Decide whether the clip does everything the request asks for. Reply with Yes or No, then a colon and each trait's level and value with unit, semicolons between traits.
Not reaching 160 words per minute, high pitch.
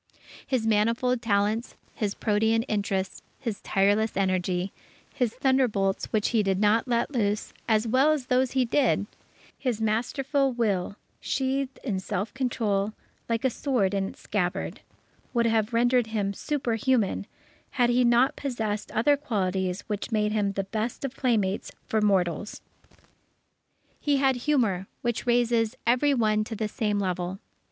Yes: average, 145 wpm; high, 220 Hz